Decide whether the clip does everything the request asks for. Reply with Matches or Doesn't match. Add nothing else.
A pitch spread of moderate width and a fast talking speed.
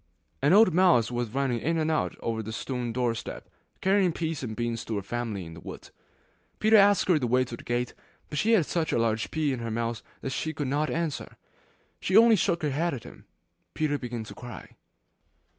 Doesn't match